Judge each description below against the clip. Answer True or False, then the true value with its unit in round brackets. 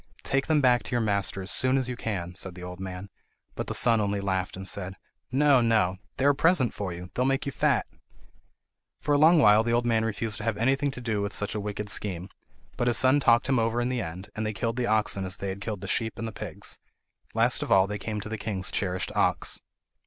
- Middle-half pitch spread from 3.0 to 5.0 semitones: True (4.0 semitones)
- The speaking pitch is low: True (110 Hz)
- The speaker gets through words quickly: True (255 wpm)